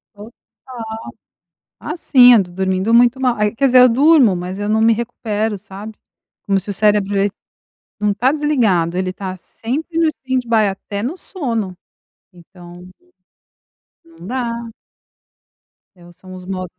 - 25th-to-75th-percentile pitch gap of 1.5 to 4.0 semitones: No, average, 4.8 semitones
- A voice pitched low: No, high, 215 Hz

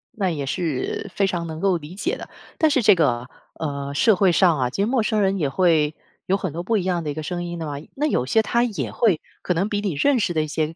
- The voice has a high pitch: No, medium, 175 Hz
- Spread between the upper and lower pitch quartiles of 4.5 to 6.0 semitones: Yes, average, 4.9 semitones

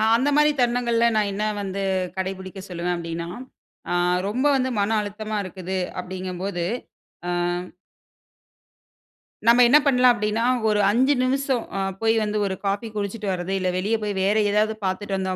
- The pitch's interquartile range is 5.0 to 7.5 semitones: No, average, 3.7 semitones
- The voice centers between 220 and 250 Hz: No, high, 205 Hz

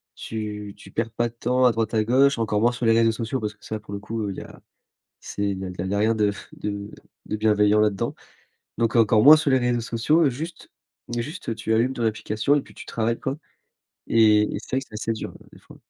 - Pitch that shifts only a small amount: Yes, narrow, 2.3 semitones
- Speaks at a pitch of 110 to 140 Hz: Yes, low, 115 Hz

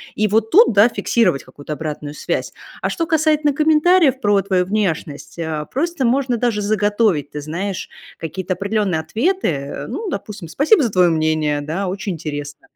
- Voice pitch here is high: Yes, high, 200 Hz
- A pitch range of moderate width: No, wide, 7.9 semitones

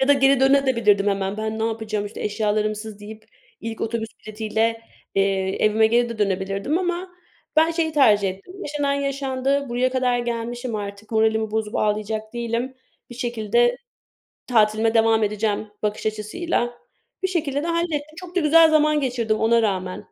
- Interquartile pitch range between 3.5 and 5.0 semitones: Yes, average, 4.3 semitones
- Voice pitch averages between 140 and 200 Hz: No, high, 225 Hz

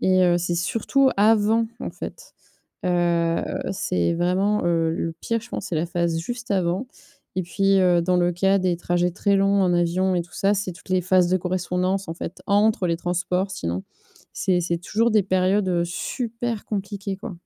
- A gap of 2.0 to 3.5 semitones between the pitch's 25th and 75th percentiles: Yes, narrow, 2.4 semitones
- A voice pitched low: No, medium, 185 Hz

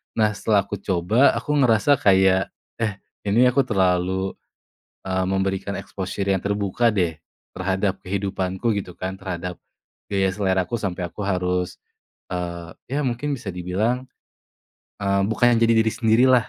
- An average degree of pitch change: Yes, average, 3.1 semitones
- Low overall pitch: Yes, very low, 95 Hz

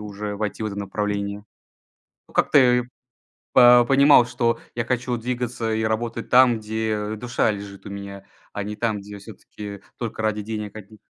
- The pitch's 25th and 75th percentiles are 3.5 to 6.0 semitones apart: No, average, 2.7 semitones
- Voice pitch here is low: Yes, low, 110 Hz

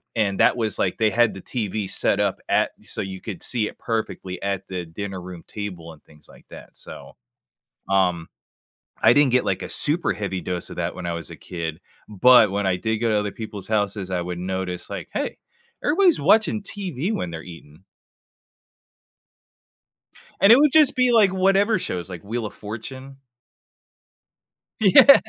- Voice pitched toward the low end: Yes, low, 105 Hz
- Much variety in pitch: Yes, wide, 5.9 semitones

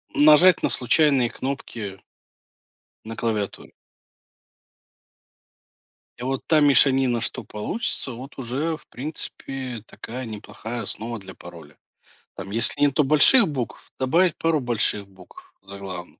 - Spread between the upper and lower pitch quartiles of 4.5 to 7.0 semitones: Yes, average, 5.3 semitones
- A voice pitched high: No, low, 125 Hz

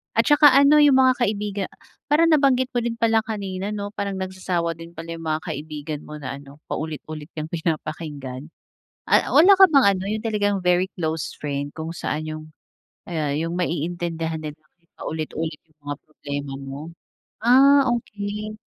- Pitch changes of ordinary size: No, wide, 5.7 semitones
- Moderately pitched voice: Yes, medium, 170 Hz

